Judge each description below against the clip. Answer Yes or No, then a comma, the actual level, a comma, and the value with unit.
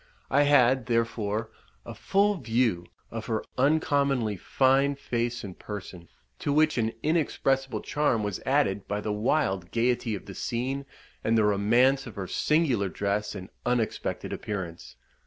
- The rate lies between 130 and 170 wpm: Yes, average, 145 wpm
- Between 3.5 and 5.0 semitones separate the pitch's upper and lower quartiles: Yes, average, 4.7 semitones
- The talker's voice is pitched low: Yes, low, 120 Hz